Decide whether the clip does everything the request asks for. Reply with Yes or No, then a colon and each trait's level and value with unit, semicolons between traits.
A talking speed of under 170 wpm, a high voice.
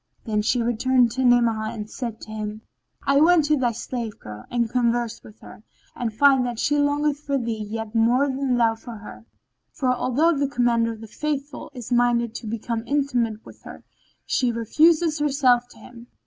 No: average, 190 wpm; high, 240 Hz